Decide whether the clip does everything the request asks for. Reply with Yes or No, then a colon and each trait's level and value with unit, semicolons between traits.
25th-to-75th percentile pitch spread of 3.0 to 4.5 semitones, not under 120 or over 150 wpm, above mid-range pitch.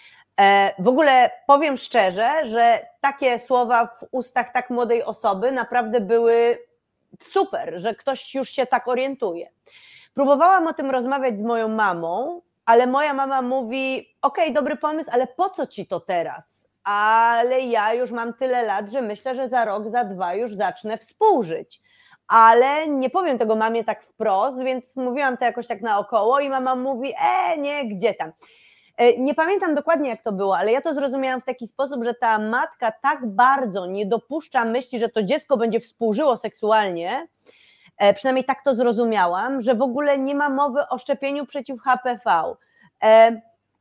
No: average, 3.4 semitones; fast, 160 wpm; very high, 255 Hz